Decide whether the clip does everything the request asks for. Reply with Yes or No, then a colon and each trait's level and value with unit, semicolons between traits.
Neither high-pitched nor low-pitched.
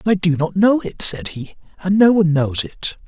Yes: medium, 180 Hz